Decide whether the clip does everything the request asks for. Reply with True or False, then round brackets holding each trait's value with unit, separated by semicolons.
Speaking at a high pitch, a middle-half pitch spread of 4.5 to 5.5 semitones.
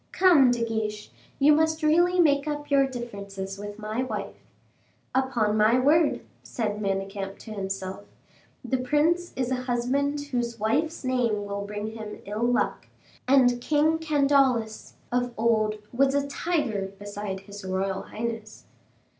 True (240 Hz; 5.2 semitones)